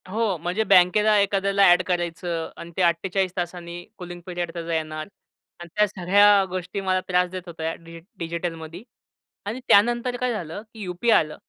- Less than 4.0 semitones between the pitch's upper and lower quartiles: Yes, average, 2.8 semitones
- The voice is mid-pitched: Yes, medium, 180 Hz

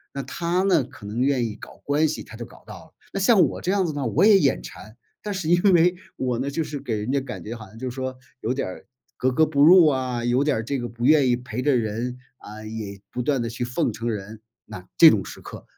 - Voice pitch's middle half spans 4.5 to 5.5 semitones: Yes, average, 5.0 semitones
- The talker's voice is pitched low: Yes, low, 130 Hz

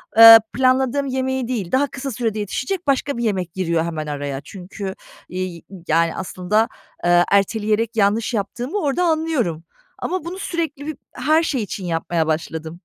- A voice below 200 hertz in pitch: No, high, 220 Hz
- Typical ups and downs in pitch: No, wide, 7.3 semitones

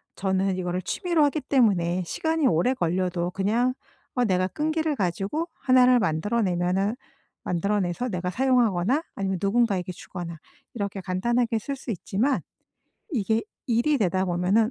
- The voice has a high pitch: Yes, high, 200 Hz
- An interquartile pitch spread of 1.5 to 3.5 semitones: No, wide, 5.5 semitones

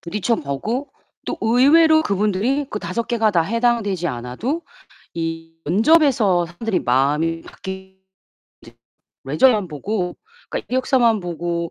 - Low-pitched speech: No, high, 195 Hz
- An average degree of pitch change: No, wide, 6.0 semitones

